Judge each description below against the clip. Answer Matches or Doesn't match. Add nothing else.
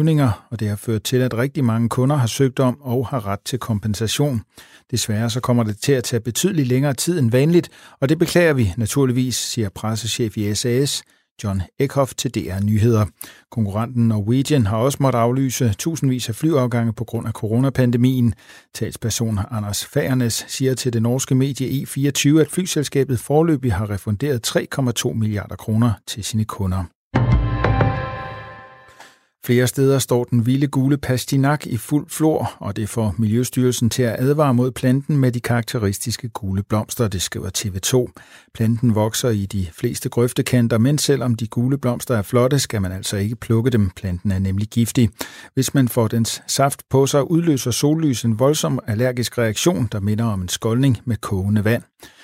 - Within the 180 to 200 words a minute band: Doesn't match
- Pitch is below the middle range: Matches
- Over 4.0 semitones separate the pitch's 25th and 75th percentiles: Doesn't match